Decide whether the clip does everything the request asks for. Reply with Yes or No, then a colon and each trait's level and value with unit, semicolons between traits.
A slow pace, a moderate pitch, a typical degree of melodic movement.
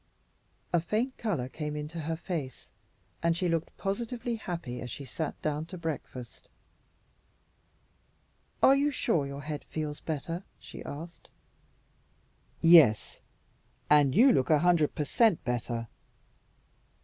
Yes: slow, 125 wpm; medium, 160 Hz; average, 3.8 semitones